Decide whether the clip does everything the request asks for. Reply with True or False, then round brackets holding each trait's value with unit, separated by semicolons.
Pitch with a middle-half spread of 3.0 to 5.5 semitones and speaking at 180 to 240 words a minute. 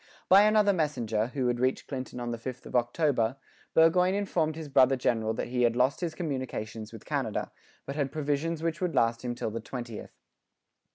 True (5.1 semitones; 185 wpm)